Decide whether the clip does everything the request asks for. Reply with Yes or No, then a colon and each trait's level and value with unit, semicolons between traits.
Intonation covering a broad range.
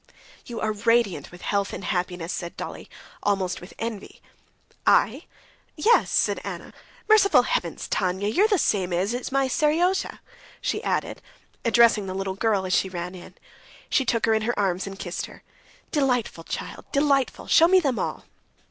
Yes: wide, 6.3 semitones